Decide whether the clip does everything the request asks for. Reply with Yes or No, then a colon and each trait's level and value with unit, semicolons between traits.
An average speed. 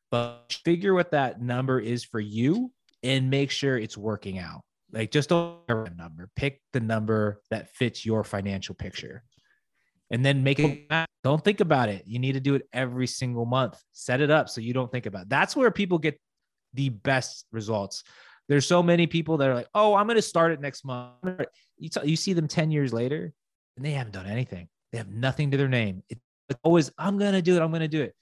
No: fast, 220 wpm